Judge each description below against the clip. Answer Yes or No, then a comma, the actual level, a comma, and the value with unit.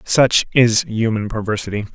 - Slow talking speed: Yes, slow, 125 wpm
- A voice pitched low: Yes, low, 110 Hz